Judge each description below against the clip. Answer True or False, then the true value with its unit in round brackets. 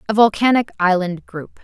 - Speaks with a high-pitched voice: True (200 Hz)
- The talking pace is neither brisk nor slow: True (145 wpm)